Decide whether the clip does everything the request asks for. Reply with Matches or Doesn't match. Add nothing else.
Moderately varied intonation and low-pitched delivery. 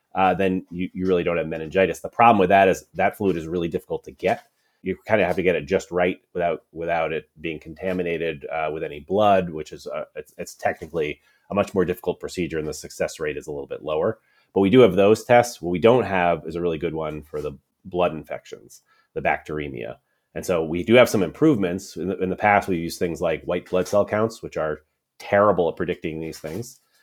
Matches